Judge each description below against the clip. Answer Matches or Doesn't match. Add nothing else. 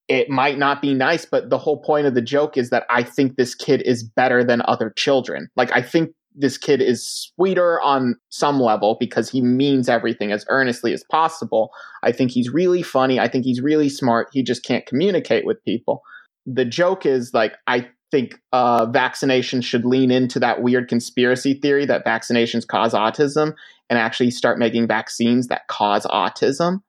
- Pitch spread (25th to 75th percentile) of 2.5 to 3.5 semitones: Matches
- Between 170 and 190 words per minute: Matches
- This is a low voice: Matches